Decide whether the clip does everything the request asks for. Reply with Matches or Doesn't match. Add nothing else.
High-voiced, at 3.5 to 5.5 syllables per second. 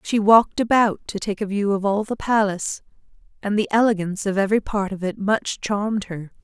Doesn't match